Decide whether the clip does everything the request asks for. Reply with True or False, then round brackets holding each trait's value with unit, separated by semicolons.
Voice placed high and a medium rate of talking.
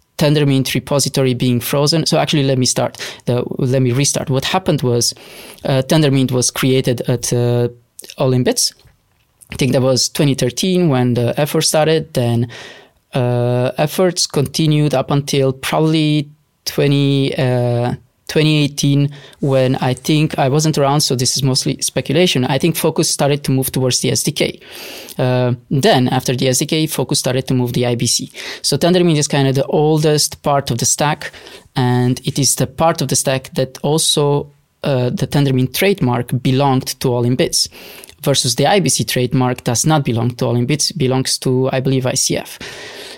False (135 Hz; 165 wpm)